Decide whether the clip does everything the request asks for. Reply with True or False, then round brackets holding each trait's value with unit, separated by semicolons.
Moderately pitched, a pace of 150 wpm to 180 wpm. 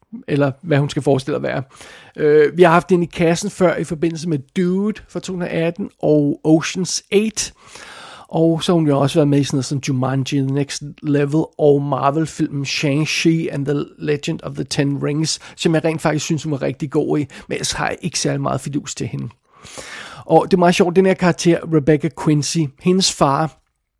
False (155 Hz; 210 wpm)